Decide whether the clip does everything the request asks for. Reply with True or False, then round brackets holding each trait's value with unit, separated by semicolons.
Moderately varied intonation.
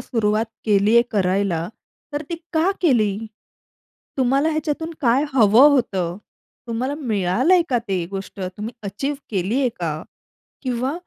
False (5.7 semitones)